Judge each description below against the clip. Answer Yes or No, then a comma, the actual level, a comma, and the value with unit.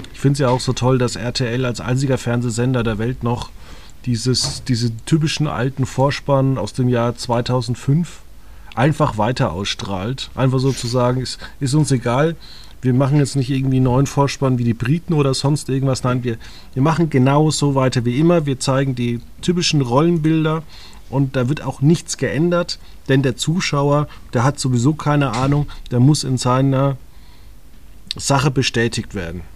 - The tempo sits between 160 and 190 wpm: Yes, average, 170 wpm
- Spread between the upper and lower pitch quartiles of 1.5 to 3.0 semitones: Yes, average, 2.7 semitones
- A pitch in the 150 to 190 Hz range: No, low, 130 Hz